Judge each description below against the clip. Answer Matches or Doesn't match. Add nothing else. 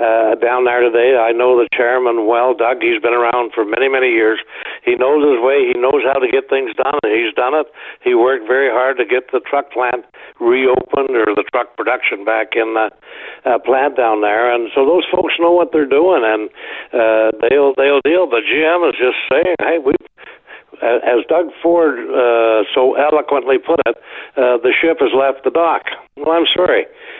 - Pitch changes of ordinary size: Doesn't match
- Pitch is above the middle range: Doesn't match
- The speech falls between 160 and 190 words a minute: Doesn't match